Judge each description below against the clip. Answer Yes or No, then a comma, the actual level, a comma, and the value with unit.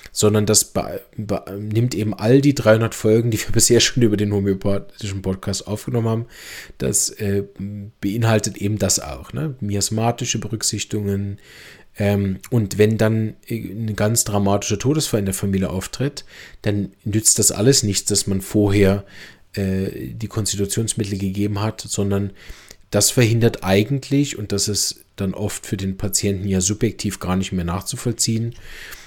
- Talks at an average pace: Yes, average, 150 wpm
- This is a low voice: Yes, low, 105 Hz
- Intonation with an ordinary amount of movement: No, narrow, 2.3 semitones